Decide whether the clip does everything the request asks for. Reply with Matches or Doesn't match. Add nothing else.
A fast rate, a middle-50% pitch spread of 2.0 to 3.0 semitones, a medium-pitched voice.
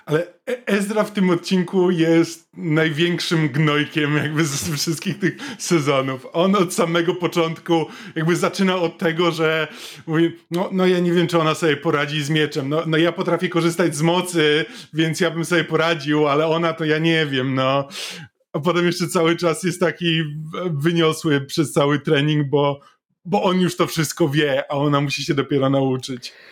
Matches